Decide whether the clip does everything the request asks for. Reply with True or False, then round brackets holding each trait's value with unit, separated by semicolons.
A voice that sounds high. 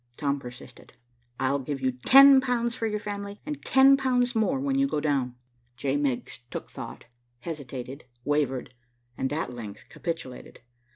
False (150 Hz)